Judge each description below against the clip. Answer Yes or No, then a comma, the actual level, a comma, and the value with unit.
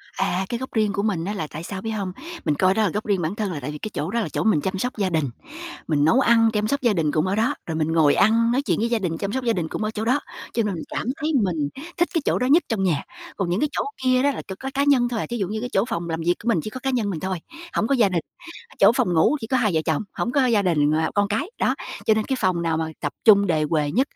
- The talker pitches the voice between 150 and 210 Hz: Yes, high, 205 Hz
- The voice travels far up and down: Yes, wide, 5.8 semitones